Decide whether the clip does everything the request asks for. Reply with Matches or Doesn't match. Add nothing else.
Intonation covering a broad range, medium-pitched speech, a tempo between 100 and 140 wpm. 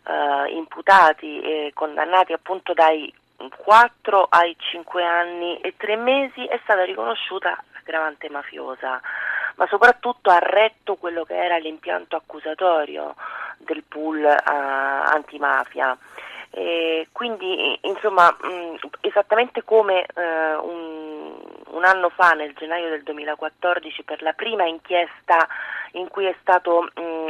Doesn't match